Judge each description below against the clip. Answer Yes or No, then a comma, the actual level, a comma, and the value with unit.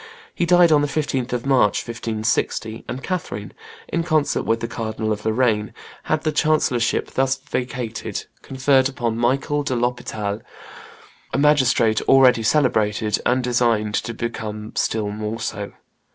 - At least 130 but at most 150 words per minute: Yes, average, 140 wpm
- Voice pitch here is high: No, low, 120 Hz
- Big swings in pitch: No, average, 3.6 semitones